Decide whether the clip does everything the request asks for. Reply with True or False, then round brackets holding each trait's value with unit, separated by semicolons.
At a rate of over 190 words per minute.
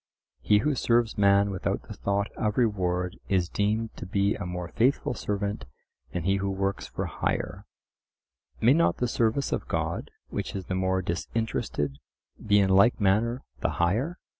False (165 wpm)